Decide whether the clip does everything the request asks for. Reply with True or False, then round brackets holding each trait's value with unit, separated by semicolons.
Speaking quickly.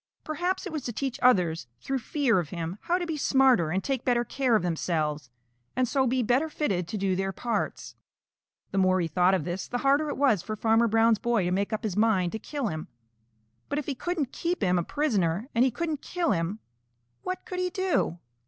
True (220 wpm)